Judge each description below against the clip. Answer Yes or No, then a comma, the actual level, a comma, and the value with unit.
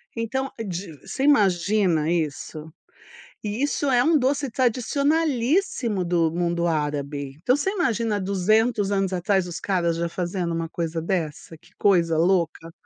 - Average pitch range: No, wide, 6.0 semitones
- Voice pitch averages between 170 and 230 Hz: Yes, high, 190 Hz